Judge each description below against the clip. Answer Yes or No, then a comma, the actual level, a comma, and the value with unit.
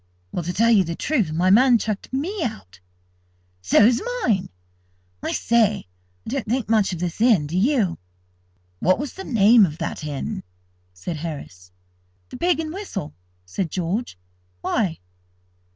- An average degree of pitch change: No, wide, 6.4 semitones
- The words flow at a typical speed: Yes, average, 150 wpm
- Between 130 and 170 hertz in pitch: No, high, 200 Hz